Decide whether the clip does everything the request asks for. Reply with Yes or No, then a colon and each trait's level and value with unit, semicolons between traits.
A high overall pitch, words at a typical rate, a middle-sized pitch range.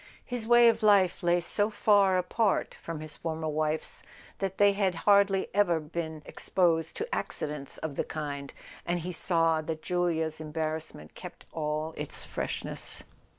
No: medium, 165 Hz; average, 150 wpm; average, 3.9 semitones